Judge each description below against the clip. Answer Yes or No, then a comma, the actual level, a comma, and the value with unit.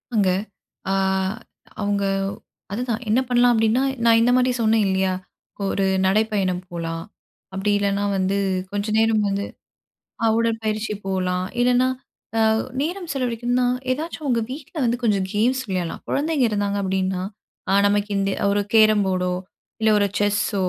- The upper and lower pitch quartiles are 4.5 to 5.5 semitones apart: No, average, 3.7 semitones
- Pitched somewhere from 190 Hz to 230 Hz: Yes, high, 210 Hz